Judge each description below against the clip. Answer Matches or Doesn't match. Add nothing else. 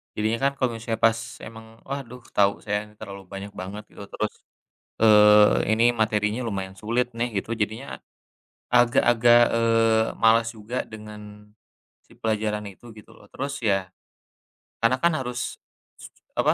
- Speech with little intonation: Matches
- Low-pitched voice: Matches